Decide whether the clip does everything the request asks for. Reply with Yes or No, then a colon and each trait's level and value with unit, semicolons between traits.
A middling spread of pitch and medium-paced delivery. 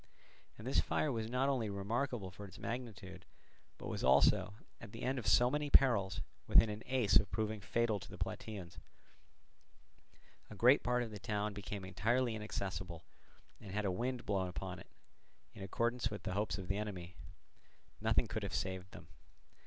Yes: average, 3.8 semitones; average, 175 wpm